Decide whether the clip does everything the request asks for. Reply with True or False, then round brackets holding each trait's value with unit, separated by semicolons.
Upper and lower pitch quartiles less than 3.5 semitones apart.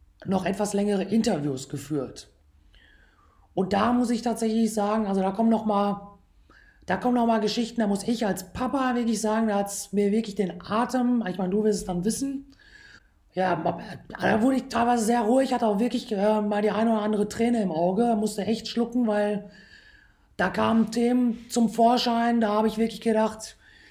True (2.7 semitones)